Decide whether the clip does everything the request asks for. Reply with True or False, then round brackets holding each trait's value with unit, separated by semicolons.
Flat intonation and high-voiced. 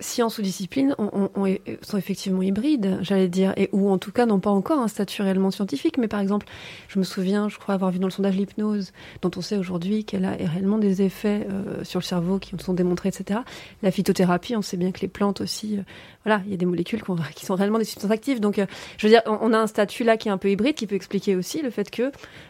True (2.1 semitones; 200 Hz)